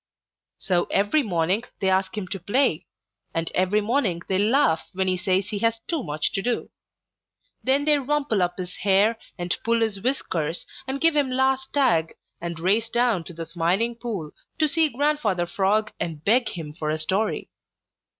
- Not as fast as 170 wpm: No, average, 180 wpm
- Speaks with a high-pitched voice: Yes, high, 205 Hz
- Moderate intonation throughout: No, wide, 5.9 semitones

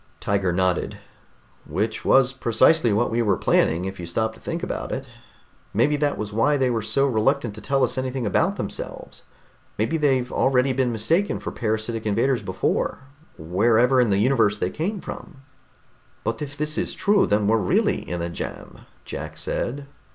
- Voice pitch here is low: Yes, low, 115 Hz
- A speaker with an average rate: Yes, average, 175 wpm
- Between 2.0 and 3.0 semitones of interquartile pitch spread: No, average, 4.6 semitones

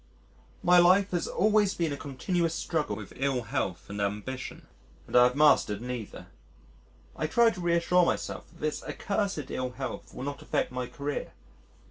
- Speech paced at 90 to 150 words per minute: No, average, 165 wpm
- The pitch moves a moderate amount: No, wide, 5.9 semitones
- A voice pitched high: No, medium, 145 Hz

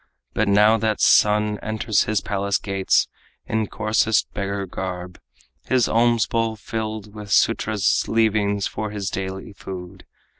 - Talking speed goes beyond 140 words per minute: No, slow, 135 wpm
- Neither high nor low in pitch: No, low, 105 Hz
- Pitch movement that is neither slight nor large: No, narrow, 1.8 semitones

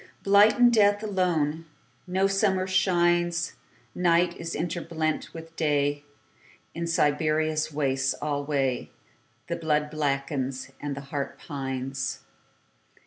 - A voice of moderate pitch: Yes, medium, 155 Hz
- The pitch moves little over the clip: No, average, 3.3 semitones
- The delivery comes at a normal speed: No, slow, 85 wpm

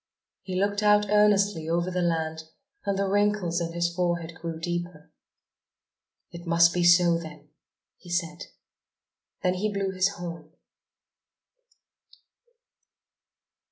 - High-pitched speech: No, medium, 175 Hz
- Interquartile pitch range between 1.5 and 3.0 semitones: Yes, narrow, 2.6 semitones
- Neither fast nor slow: No, slow, 120 wpm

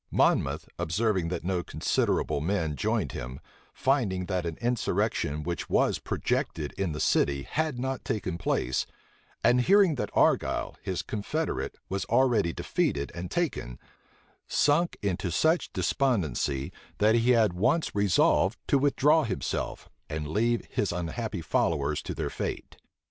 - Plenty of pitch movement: Yes, wide, 6.9 semitones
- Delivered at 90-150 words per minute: Yes, average, 140 wpm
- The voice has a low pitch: Yes, low, 100 Hz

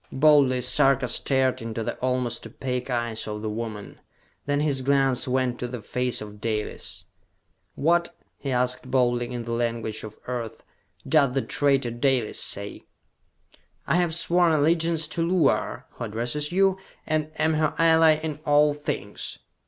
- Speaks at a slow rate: No, average, 155 wpm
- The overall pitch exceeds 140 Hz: No, low, 130 Hz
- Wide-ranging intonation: No, average, 4.3 semitones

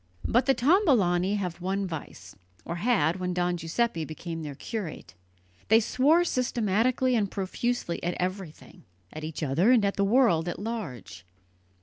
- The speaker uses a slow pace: No, average, 150 wpm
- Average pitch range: No, wide, 6.2 semitones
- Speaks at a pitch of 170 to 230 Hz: Yes, high, 190 Hz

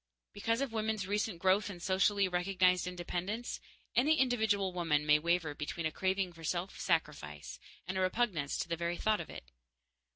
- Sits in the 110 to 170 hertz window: No, medium, 185 Hz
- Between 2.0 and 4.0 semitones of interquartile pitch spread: Yes, average, 3.4 semitones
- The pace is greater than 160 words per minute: Yes, average, 170 wpm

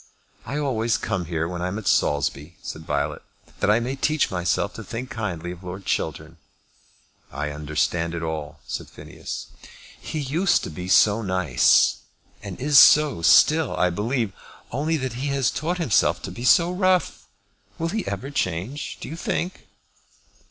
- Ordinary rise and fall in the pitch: No, wide, 8.9 semitones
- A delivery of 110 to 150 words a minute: No, average, 165 wpm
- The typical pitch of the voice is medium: No, low, 110 Hz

